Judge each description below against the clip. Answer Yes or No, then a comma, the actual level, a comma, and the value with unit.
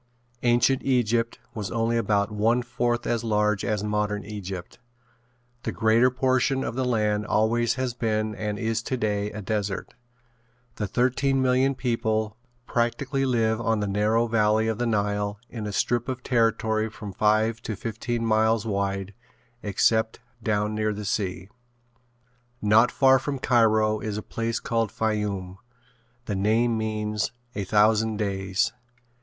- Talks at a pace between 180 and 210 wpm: No, average, 145 wpm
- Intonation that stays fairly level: Yes, narrow, 2.0 semitones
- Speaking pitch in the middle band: No, low, 110 Hz